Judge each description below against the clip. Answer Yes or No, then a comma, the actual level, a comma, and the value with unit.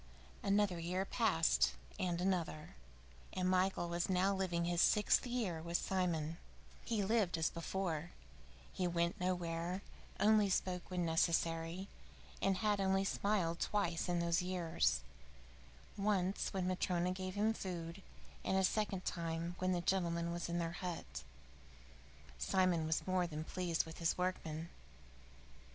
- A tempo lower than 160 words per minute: Yes, average, 140 wpm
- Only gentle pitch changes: Yes, narrow, 2.2 semitones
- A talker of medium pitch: Yes, medium, 180 Hz